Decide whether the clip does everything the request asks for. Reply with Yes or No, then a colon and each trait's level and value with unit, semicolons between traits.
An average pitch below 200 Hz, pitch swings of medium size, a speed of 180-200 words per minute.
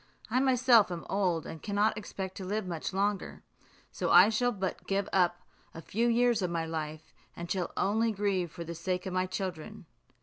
Yes: high, 190 Hz; average, 3.6 semitones; average, 195 wpm